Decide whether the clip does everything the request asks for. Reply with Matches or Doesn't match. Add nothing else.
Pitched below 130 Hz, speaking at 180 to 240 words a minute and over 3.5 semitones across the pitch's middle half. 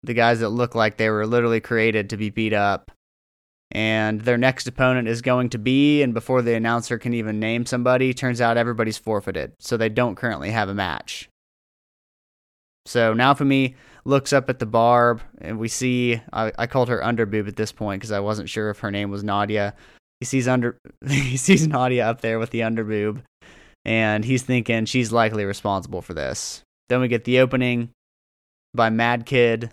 Doesn't match